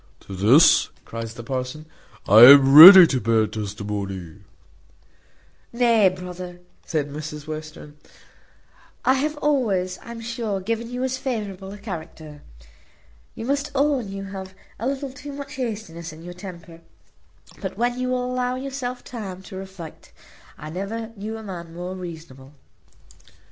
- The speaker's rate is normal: Yes, average, 145 wpm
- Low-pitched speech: No, high, 190 Hz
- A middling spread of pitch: No, wide, 7.4 semitones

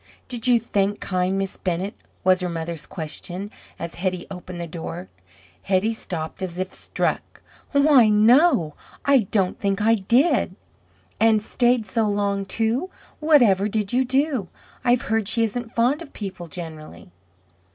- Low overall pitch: No, high, 205 Hz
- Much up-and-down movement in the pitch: No, average, 4.5 semitones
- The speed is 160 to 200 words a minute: No, average, 150 wpm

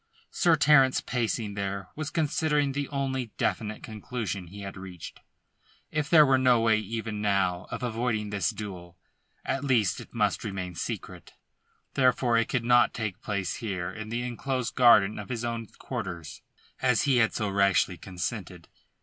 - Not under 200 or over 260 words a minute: No, average, 160 wpm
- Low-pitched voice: Yes, low, 110 Hz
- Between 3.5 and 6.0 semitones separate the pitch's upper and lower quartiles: Yes, average, 4.5 semitones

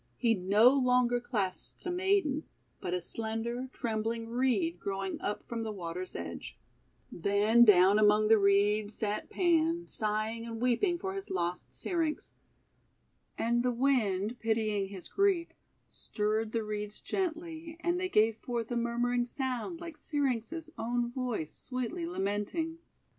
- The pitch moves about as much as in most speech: Yes, average, 5.0 semitones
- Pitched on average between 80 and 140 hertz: No, high, 230 Hz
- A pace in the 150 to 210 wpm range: No, average, 140 wpm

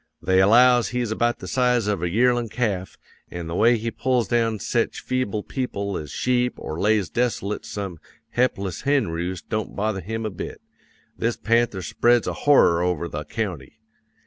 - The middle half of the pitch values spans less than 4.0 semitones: No, average, 4.5 semitones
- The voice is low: Yes, low, 110 Hz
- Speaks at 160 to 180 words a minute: Yes, average, 170 wpm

